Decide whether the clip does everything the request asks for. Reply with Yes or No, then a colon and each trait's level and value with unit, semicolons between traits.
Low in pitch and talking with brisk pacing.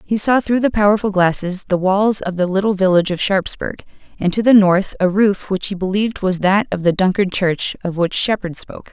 No: high, 195 Hz; fast, 220 wpm